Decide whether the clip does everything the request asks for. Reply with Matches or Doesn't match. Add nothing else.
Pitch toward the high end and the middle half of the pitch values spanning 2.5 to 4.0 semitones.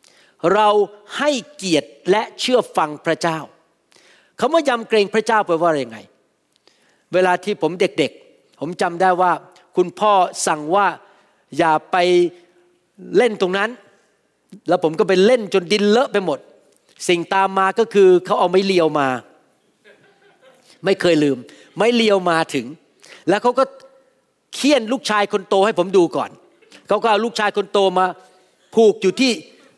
Matches